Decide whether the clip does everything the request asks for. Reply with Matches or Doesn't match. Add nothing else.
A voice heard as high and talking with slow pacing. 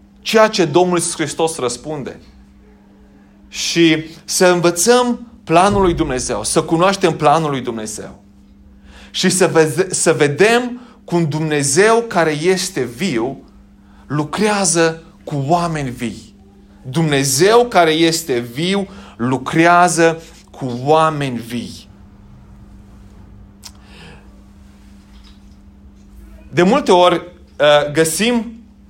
Doesn't match